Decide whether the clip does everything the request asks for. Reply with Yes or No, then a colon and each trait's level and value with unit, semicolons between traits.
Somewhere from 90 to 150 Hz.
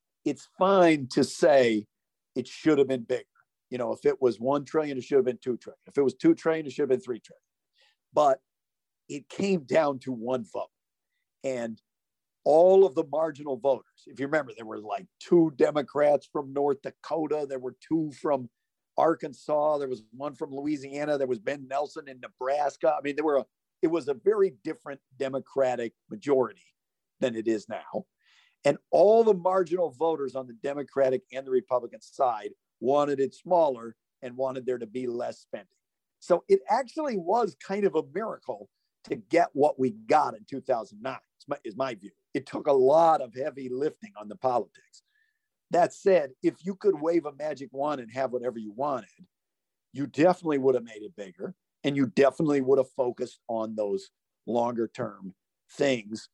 Yes: medium, 140 Hz